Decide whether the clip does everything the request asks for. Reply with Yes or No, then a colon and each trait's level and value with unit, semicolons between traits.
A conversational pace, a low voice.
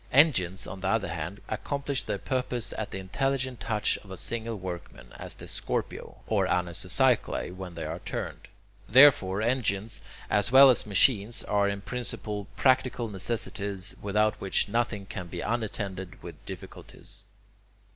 Yes: average, 145 wpm; low, 105 Hz